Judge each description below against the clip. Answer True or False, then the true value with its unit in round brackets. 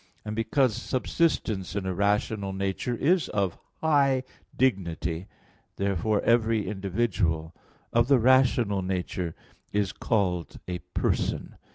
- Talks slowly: True (110 wpm)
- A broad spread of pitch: False (4.2 semitones)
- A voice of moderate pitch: False (100 Hz)